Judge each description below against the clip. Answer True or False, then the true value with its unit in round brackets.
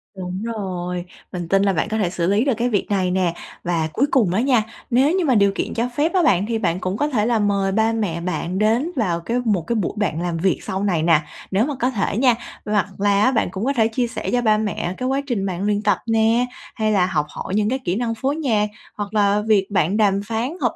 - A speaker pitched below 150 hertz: False (210 Hz)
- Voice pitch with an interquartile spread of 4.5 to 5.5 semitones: False (3.8 semitones)